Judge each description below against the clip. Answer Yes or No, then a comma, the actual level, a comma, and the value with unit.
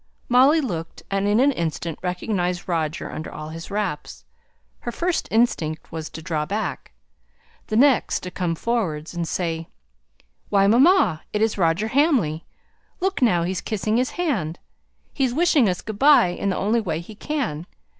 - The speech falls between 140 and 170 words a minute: Yes, average, 160 wpm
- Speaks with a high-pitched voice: Yes, high, 195 Hz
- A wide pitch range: Yes, wide, 6.5 semitones